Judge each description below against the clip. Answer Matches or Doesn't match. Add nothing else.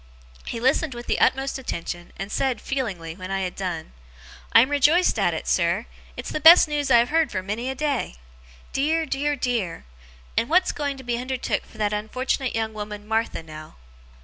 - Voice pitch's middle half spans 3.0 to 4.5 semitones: Doesn't match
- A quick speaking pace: Doesn't match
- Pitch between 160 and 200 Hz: Doesn't match